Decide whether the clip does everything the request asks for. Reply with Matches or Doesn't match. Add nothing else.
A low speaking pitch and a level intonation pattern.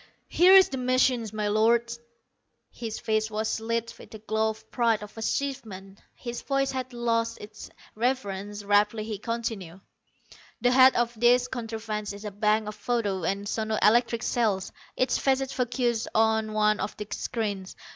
Doesn't match